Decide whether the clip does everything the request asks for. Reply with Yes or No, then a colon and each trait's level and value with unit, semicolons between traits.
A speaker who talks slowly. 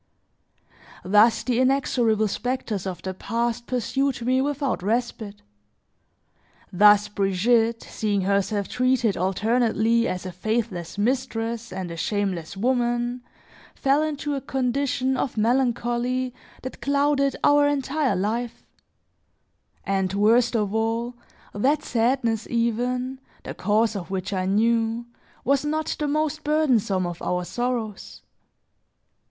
Yes: slow, 115 wpm